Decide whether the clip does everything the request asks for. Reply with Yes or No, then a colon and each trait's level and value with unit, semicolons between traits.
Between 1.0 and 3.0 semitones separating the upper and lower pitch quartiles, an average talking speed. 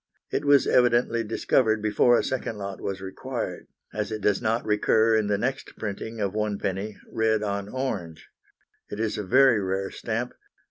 Yes: narrow, 2.4 semitones; average, 170 wpm